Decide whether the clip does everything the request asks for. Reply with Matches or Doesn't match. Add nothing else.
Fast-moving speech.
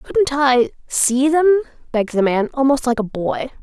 Doesn't match